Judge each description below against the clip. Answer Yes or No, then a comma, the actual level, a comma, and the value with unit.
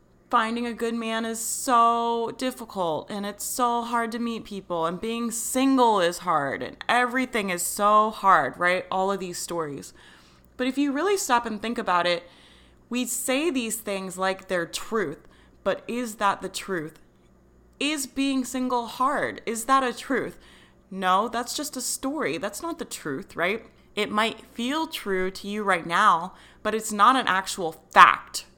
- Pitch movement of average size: Yes, average, 4.6 semitones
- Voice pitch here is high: Yes, high, 225 Hz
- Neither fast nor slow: Yes, average, 170 wpm